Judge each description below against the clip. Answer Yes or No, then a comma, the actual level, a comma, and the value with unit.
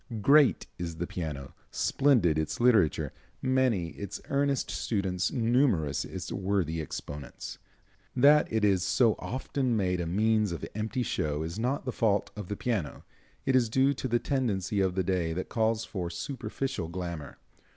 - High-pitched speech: No, low, 105 Hz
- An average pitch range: No, wide, 6.2 semitones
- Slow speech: No, average, 160 wpm